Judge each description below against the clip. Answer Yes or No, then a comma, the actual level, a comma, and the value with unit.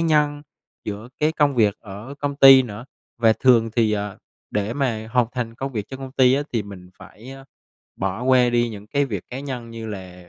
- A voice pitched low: Yes, low, 120 Hz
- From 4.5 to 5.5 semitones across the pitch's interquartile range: No, average, 4.1 semitones